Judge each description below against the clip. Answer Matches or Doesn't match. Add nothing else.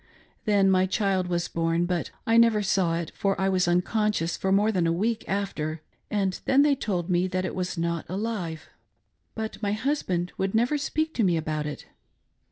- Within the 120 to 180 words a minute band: Doesn't match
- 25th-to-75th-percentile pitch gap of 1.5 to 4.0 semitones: Matches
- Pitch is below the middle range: Doesn't match